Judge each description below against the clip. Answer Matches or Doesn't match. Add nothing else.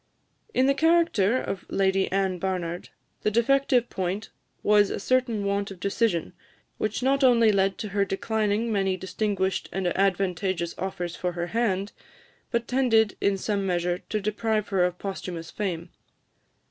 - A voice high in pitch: Matches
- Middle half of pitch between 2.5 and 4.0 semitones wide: Matches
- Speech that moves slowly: Doesn't match